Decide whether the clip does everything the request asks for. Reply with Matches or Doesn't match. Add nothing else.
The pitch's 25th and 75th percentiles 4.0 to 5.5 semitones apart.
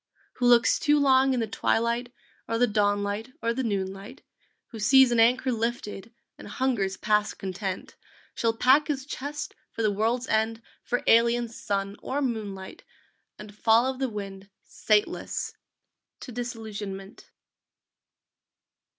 Doesn't match